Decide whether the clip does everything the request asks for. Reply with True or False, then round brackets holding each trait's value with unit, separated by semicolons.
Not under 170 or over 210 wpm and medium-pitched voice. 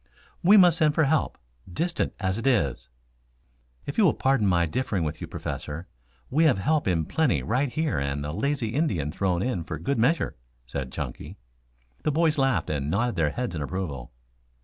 False (185 wpm; 115 Hz)